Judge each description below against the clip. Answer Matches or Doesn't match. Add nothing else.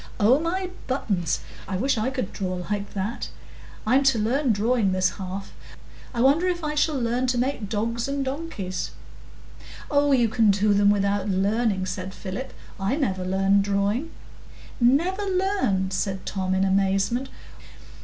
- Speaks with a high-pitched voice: Matches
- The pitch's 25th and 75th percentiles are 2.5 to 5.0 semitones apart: Doesn't match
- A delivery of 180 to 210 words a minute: Doesn't match